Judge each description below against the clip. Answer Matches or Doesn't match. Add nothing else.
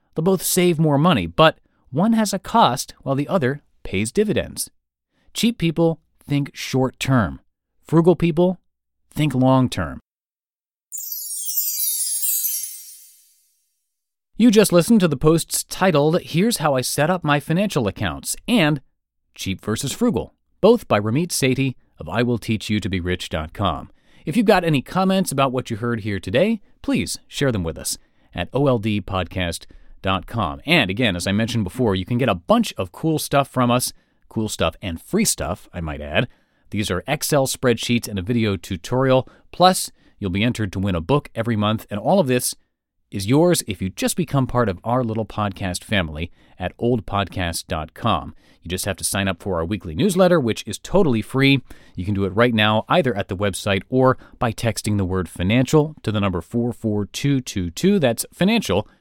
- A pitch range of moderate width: Doesn't match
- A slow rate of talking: Doesn't match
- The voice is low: Matches